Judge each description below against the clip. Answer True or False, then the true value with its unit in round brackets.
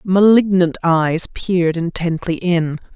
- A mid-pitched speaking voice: True (175 Hz)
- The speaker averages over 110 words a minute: False (100 wpm)